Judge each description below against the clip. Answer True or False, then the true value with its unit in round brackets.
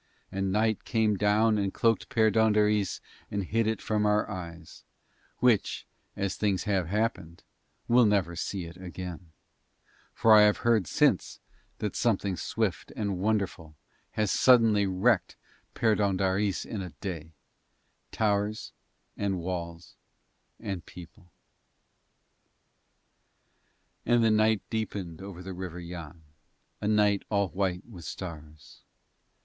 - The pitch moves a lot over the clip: False (3.2 semitones)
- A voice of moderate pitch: False (100 Hz)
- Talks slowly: True (120 wpm)